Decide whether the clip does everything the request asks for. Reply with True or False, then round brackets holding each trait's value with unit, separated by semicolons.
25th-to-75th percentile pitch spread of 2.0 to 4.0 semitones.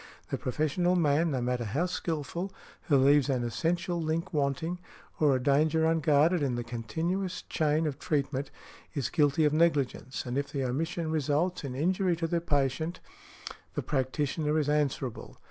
True (3.3 semitones)